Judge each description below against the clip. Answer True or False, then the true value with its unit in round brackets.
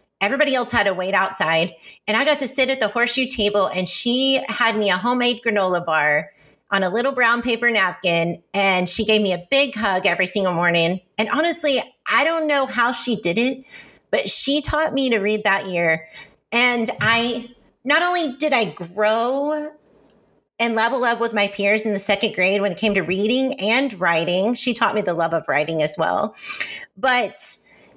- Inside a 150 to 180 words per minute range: False (195 wpm)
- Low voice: False (220 Hz)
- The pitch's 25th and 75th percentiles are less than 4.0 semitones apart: False (5.1 semitones)